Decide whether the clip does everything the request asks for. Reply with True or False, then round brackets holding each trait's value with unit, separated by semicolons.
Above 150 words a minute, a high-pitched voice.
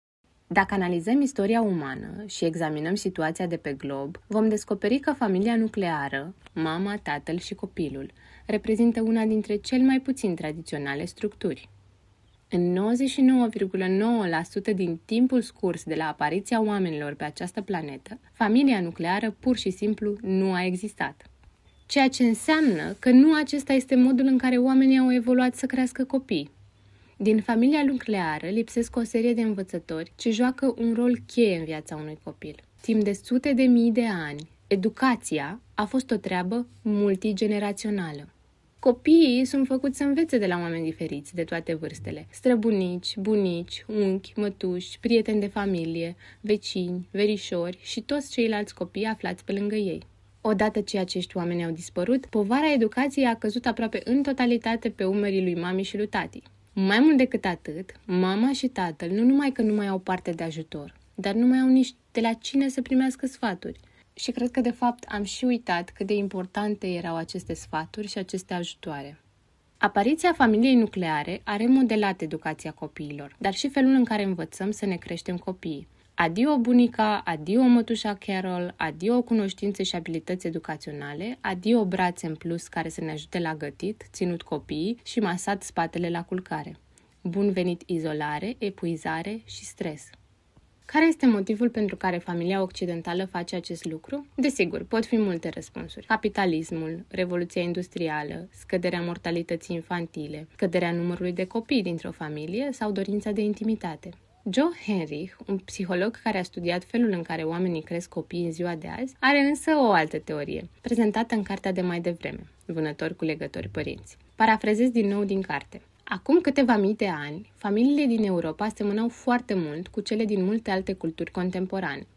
True (160 wpm; 200 Hz)